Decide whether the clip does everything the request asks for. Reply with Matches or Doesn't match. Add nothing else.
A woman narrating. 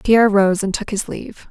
Matches